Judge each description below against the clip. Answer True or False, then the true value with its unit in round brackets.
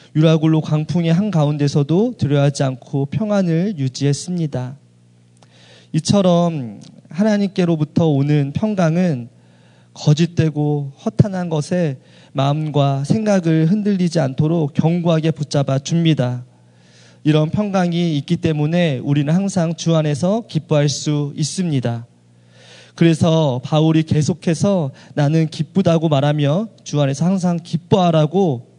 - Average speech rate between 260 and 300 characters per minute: True (275 characters per minute)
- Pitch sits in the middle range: True (155 Hz)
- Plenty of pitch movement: False (3.3 semitones)